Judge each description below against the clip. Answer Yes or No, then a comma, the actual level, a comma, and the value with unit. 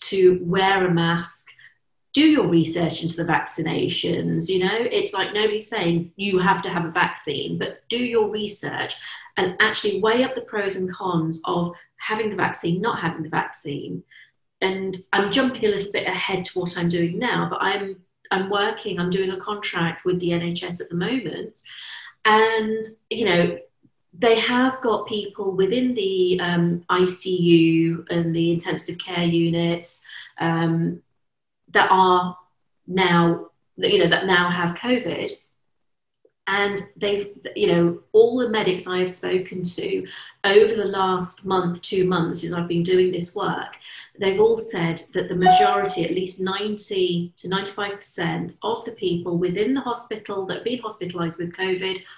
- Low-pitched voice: No, medium, 185 Hz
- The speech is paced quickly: No, average, 160 wpm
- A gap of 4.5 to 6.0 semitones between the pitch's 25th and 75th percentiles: No, average, 3.4 semitones